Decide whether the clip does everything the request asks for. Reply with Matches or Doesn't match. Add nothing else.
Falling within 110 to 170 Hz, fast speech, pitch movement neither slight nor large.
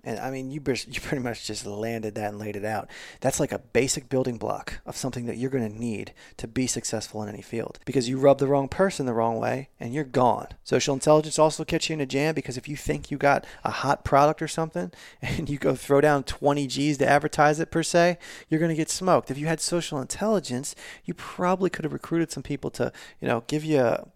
Matches